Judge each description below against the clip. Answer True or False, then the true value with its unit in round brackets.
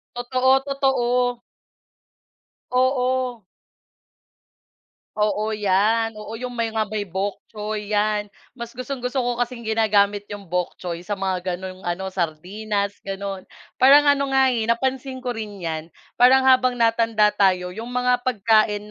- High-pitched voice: True (220 Hz)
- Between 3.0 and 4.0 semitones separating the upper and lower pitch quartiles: True (3.7 semitones)